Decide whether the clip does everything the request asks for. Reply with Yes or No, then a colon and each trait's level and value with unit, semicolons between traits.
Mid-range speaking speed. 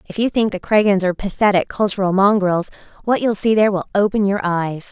No: fast, 210 wpm